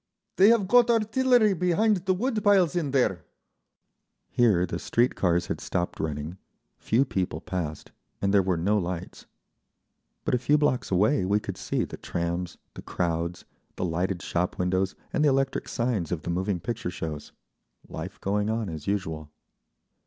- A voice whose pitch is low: Yes, low, 100 Hz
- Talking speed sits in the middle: Yes, average, 160 wpm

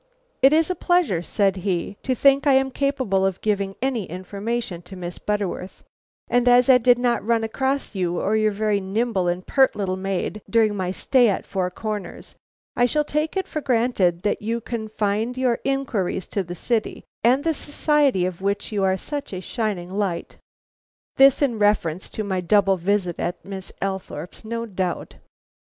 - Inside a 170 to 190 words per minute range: Yes, average, 180 wpm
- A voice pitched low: No, high, 210 Hz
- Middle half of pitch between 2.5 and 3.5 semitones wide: No, average, 4.7 semitones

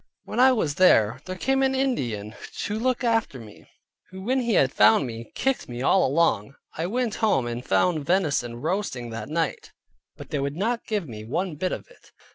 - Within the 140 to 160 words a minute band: No, average, 200 wpm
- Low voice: No, medium, 165 Hz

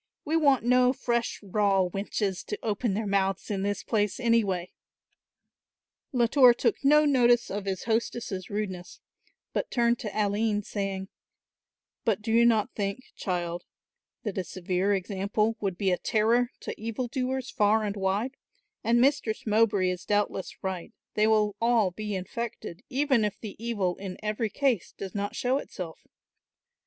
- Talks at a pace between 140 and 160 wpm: Yes, average, 155 wpm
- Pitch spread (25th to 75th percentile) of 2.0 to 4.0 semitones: Yes, average, 3.3 semitones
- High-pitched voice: Yes, high, 210 Hz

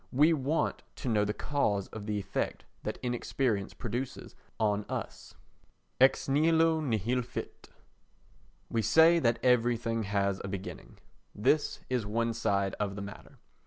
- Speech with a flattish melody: No, average, 4.5 semitones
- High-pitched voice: No, low, 115 Hz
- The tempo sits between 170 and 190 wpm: No, average, 140 wpm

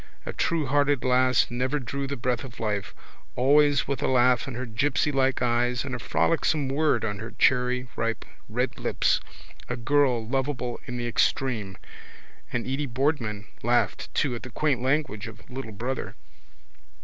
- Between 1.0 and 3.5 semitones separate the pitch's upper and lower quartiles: Yes, average, 2.7 semitones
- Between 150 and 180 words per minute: Yes, average, 155 wpm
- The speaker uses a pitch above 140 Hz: No, low, 125 Hz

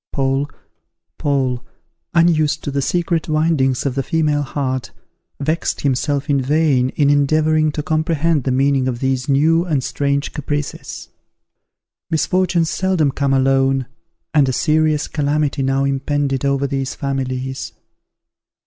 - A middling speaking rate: No, slow, 125 wpm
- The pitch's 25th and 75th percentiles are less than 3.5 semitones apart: Yes, narrow, 2.6 semitones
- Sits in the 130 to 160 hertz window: Yes, medium, 140 Hz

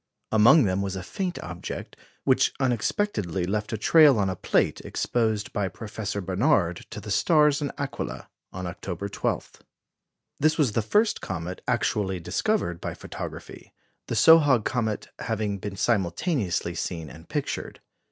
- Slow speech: No, average, 145 wpm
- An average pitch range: No, wide, 6.5 semitones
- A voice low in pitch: Yes, low, 105 Hz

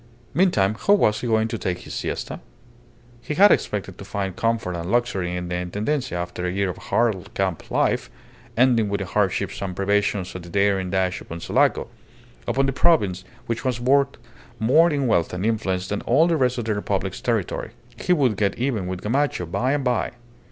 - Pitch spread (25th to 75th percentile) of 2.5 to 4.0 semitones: No, average, 5.2 semitones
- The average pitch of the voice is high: No, low, 105 Hz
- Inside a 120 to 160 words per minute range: No, average, 195 wpm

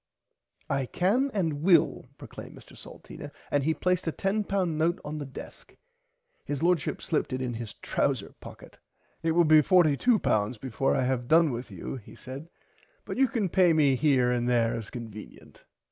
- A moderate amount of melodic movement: No, wide, 5.7 semitones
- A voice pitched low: No, medium, 150 Hz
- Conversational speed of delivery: Yes, average, 175 wpm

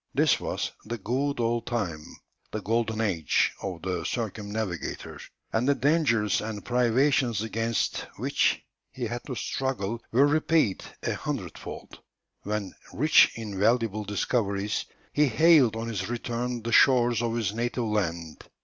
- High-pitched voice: No, low, 115 Hz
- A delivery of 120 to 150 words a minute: Yes, average, 140 wpm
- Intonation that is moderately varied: Yes, average, 3.0 semitones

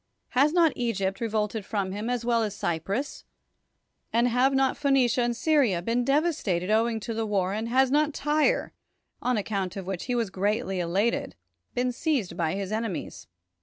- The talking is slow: No, average, 175 wpm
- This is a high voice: Yes, high, 230 Hz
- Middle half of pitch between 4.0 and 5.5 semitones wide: Yes, average, 4.3 semitones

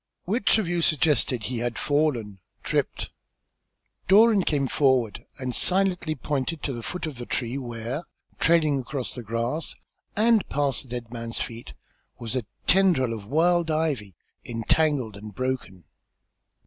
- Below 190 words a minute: Yes, average, 150 wpm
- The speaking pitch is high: No, low, 135 Hz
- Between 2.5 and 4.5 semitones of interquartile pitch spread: No, wide, 5.5 semitones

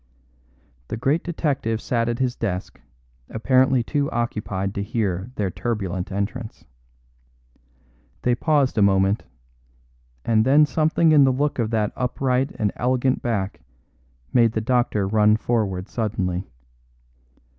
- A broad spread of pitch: No, average, 4.0 semitones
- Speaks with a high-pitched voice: No, low, 115 Hz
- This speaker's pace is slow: Yes, slow, 125 wpm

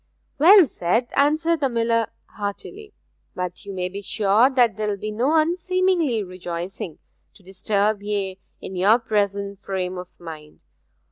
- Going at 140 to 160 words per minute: Yes, average, 145 wpm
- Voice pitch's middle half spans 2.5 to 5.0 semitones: No, wide, 5.5 semitones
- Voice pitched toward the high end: Yes, high, 210 Hz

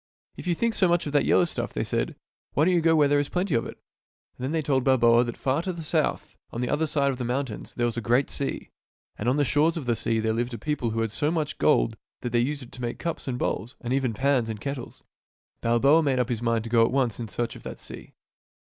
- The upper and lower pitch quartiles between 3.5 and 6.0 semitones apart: Yes, average, 4.0 semitones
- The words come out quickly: Yes, fast, 290 wpm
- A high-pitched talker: No, low, 130 Hz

